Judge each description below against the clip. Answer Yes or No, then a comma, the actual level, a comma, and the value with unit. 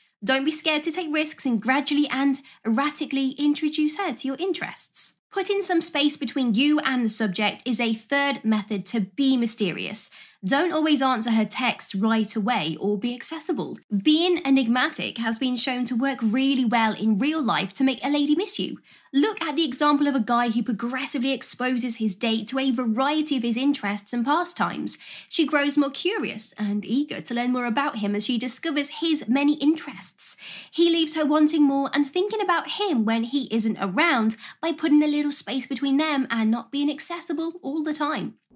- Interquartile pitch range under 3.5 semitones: No, average, 4.3 semitones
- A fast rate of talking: No, average, 190 wpm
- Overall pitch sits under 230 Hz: No, very high, 270 Hz